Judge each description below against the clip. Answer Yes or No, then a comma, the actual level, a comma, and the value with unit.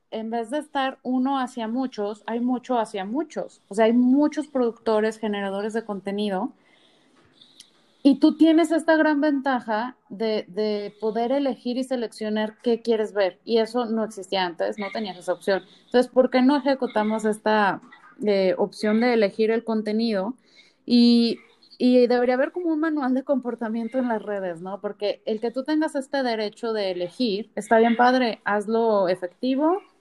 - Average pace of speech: Yes, average, 165 wpm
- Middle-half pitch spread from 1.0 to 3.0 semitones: No, average, 3.5 semitones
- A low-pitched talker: No, high, 230 Hz